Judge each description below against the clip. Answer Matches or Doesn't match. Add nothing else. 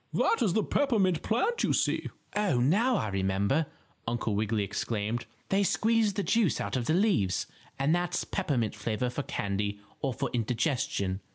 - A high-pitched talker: Doesn't match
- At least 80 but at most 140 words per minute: Doesn't match